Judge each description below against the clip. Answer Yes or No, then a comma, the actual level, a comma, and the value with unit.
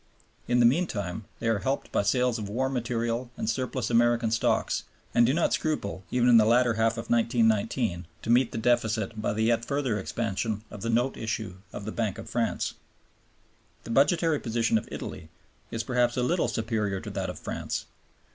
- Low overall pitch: Yes, low, 115 Hz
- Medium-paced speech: Yes, average, 190 wpm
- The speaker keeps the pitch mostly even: Yes, narrow, 2.0 semitones